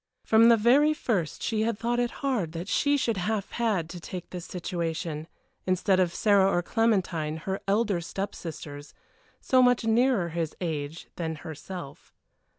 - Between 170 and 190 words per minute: No, average, 160 wpm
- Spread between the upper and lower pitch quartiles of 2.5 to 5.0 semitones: No, wide, 5.5 semitones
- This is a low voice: No, high, 190 Hz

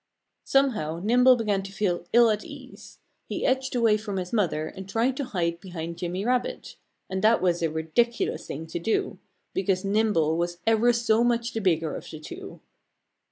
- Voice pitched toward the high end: Yes, high, 205 Hz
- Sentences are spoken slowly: No, average, 180 wpm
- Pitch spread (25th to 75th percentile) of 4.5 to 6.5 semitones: Yes, average, 5.3 semitones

